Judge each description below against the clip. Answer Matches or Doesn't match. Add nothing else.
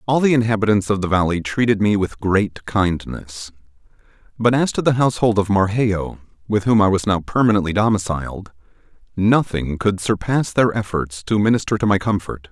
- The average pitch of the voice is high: Doesn't match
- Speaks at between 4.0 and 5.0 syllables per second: Doesn't match